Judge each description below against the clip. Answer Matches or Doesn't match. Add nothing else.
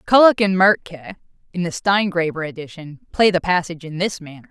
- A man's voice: Doesn't match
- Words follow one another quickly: Doesn't match